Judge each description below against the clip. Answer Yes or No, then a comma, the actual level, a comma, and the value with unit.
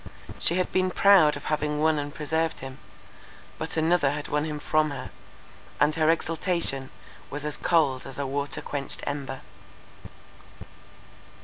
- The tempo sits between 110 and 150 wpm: Yes, average, 140 wpm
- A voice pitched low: No, medium, 150 Hz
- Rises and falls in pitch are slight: Yes, narrow, 2.3 semitones